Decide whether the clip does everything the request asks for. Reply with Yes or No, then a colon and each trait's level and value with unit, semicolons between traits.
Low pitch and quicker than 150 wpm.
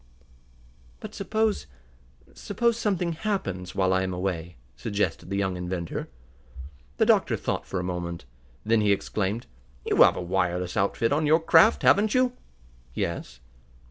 No: low, 100 Hz; average, 140 wpm